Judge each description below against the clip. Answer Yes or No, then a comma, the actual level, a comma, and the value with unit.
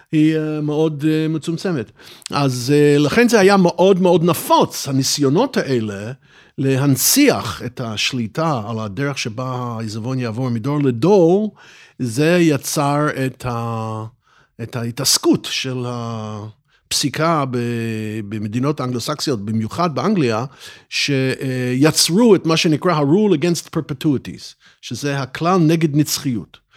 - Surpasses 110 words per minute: No, slow, 100 wpm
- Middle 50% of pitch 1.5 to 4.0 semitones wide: No, average, 4.8 semitones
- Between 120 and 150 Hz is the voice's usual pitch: Yes, medium, 140 Hz